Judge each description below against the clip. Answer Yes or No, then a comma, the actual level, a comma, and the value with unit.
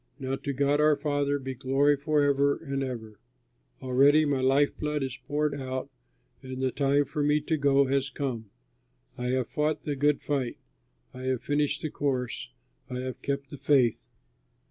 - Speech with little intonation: Yes, narrow, 1.9 semitones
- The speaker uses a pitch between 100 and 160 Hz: Yes, medium, 140 Hz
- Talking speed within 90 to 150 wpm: No, average, 170 wpm